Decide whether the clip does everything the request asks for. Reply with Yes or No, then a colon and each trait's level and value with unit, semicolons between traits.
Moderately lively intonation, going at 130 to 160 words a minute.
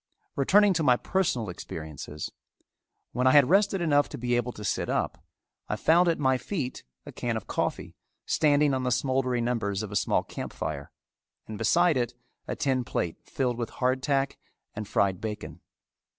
No: average, 4.8 semitones; average, 180 wpm